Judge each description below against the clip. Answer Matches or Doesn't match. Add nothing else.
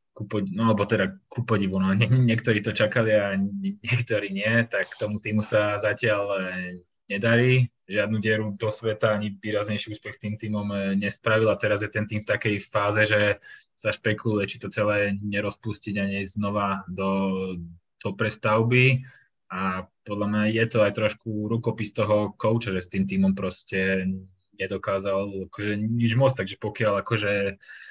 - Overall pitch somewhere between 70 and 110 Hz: Matches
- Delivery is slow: Doesn't match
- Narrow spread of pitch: Matches